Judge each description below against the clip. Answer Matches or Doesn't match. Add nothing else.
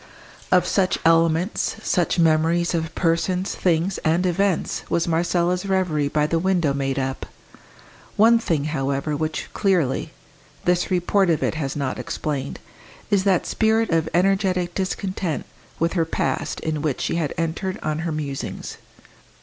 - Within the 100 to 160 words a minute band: Matches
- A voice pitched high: Doesn't match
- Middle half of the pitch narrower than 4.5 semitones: Matches